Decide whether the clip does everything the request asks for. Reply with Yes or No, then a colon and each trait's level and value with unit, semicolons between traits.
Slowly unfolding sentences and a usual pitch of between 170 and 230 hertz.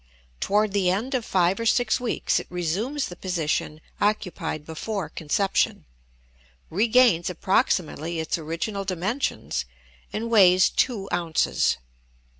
Yes: slow, 115 wpm; high, 190 Hz